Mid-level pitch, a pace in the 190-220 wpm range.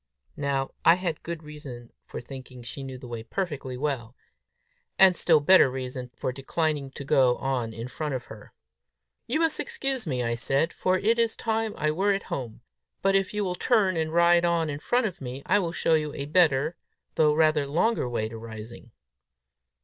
Yes: medium, 150 Hz; average, 195 wpm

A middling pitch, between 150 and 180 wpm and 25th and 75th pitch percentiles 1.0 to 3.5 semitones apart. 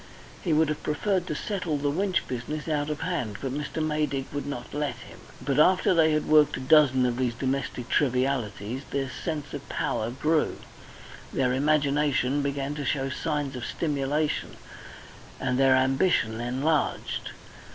Yes: medium, 145 Hz; average, 160 wpm; average, 2.8 semitones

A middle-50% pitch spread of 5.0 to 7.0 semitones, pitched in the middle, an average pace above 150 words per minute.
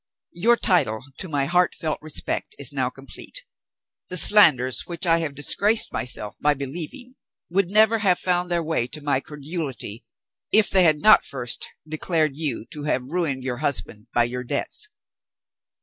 Yes: average, 5.3 semitones; medium, 155 Hz; average, 165 wpm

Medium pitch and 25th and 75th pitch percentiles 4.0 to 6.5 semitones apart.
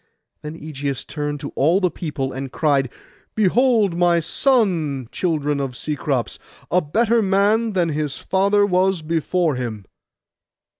Yes: medium, 165 Hz; average, 5.0 semitones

